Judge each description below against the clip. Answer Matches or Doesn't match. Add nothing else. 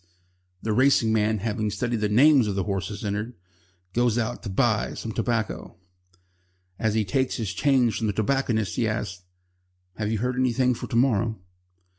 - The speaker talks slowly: Doesn't match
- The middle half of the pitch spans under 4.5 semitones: Matches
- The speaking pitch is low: Matches